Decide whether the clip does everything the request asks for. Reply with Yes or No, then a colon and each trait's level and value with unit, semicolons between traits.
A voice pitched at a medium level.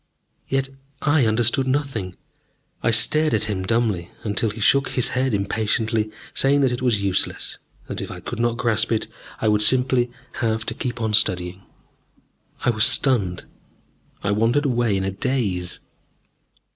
No: low, 115 Hz